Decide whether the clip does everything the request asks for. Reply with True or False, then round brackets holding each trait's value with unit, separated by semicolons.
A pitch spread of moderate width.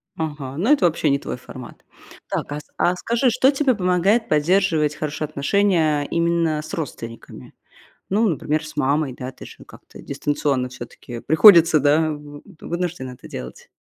True (3.9 semitones)